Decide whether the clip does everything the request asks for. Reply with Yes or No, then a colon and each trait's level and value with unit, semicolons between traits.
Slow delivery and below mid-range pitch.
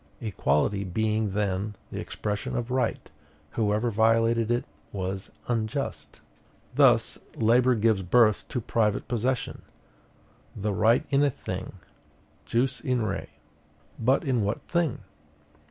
Yes: slow, 120 wpm; low, 110 Hz